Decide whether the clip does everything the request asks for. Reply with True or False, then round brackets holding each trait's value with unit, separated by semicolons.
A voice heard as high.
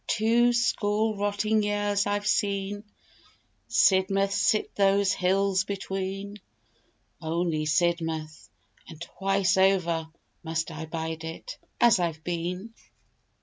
True (195 Hz)